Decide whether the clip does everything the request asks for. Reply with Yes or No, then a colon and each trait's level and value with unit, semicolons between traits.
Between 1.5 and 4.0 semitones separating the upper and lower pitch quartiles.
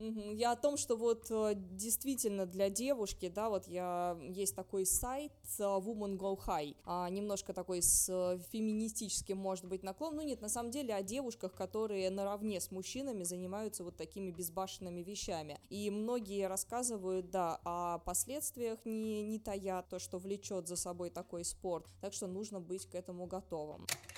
Yes: average, 3.2 semitones